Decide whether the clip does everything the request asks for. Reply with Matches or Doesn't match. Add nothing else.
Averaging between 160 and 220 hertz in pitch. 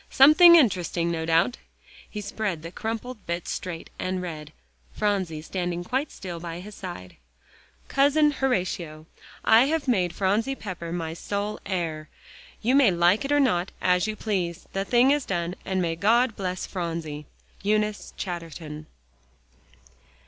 Matches